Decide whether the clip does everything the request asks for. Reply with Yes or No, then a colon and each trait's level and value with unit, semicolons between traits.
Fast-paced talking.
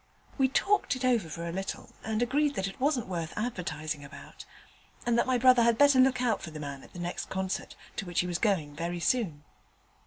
Yes: fast, 220 wpm